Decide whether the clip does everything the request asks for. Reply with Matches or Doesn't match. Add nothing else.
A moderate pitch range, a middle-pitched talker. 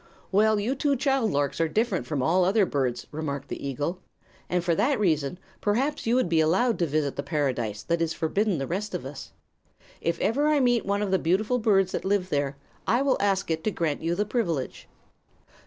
Doesn't match